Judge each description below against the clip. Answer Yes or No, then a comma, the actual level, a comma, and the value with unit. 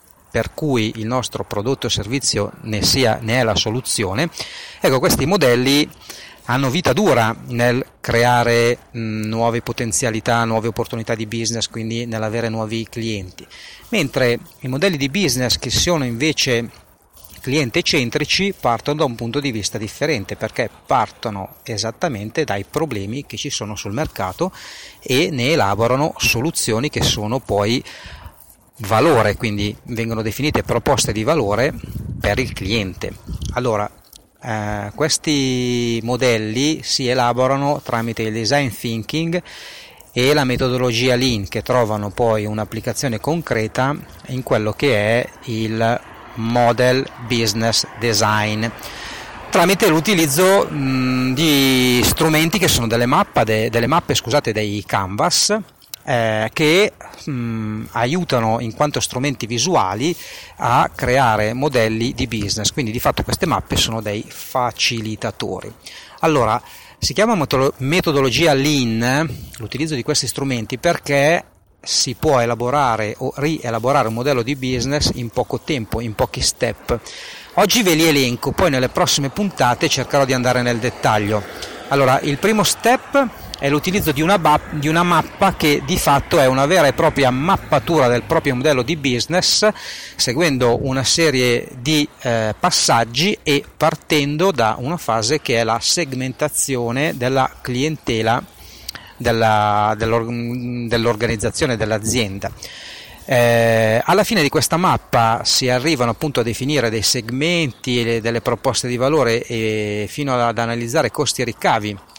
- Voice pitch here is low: Yes, low, 125 Hz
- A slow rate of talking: No, average, 130 wpm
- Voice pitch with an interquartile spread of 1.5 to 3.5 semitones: No, average, 4.2 semitones